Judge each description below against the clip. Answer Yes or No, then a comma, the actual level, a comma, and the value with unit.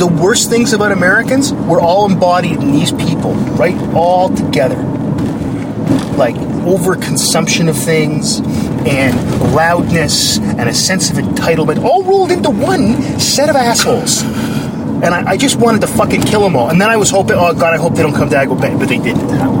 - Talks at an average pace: Yes, average, 175 wpm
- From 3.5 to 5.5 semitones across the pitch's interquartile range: Yes, average, 4.5 semitones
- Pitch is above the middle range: Yes, high, 205 Hz